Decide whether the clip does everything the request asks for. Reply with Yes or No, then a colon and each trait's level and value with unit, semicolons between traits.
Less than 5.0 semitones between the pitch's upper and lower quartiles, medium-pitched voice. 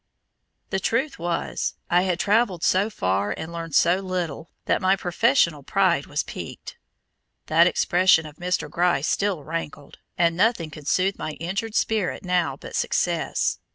Yes: average, 3.0 semitones; medium, 175 Hz